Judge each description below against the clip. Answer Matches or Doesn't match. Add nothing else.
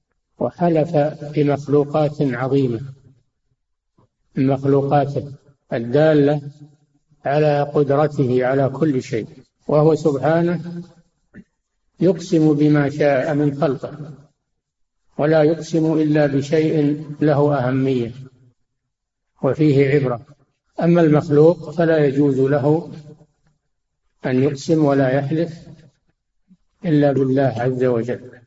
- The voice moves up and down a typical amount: Doesn't match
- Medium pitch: Matches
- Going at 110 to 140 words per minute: Doesn't match